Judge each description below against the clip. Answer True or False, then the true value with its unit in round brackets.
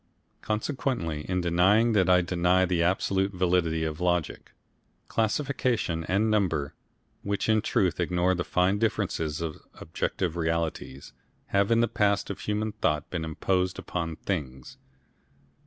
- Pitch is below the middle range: True (90 Hz)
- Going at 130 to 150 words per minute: True (135 wpm)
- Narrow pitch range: False (3.7 semitones)